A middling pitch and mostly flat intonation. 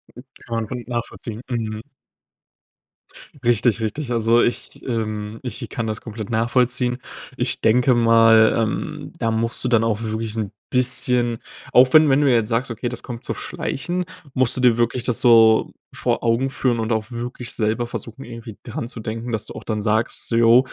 No: low, 115 Hz; narrow, 1.8 semitones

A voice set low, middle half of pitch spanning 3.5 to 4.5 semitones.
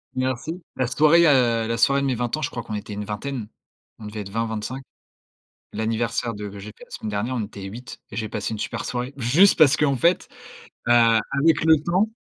Yes: low, 120 Hz; average, 4.2 semitones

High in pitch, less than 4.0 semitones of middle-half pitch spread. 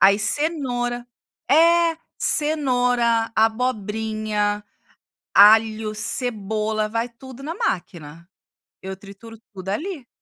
Yes: high, 225 Hz; average, 3.4 semitones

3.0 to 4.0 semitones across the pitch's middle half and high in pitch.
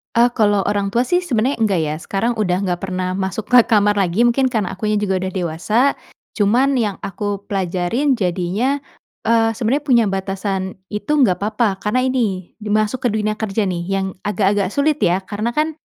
Yes: average, 3.5 semitones; high, 210 Hz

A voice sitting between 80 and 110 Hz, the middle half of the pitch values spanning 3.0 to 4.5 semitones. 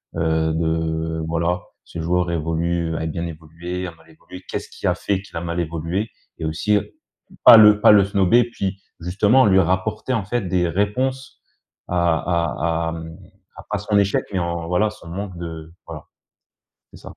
Yes: very low, 85 Hz; average, 3.3 semitones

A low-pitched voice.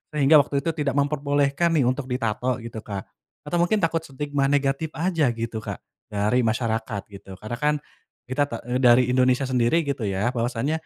Yes: low, 130 Hz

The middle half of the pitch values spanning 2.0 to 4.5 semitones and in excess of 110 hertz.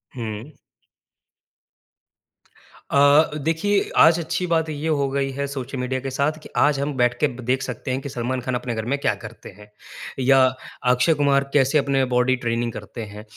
Yes: average, 2.8 semitones; low, 135 Hz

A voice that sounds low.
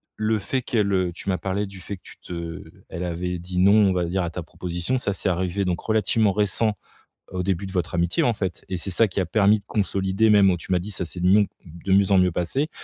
Yes: very low, 95 Hz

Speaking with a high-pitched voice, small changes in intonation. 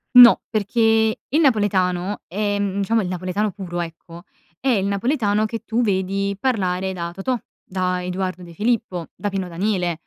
No: high, 195 Hz; average, 3.1 semitones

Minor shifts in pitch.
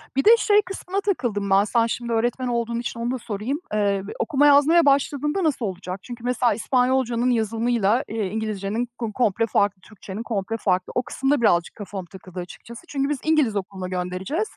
No: average, 4.8 semitones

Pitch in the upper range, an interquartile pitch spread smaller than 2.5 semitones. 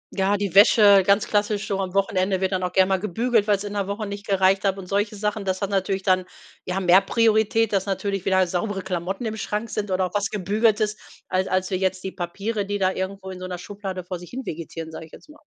Yes: high, 195 Hz; narrow, 1.8 semitones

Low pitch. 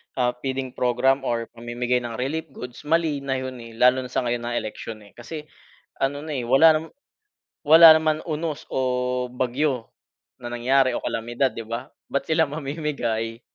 Yes: low, 130 Hz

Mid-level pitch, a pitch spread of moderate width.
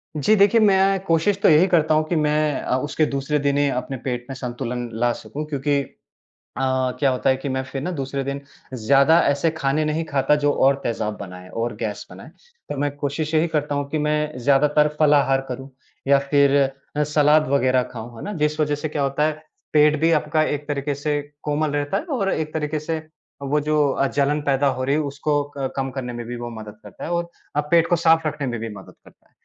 No: medium, 145 Hz; narrow, 2.3 semitones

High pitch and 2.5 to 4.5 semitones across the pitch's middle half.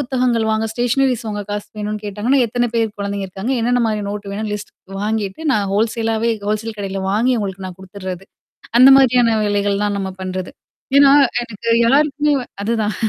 Yes: high, 215 Hz; average, 3.1 semitones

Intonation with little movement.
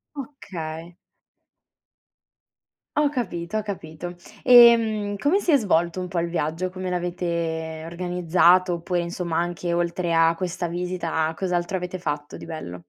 Yes: narrow, 1.9 semitones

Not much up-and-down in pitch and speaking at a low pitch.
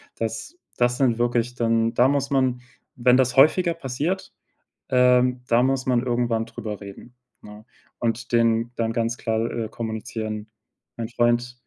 Yes: narrow, 1.7 semitones; low, 120 Hz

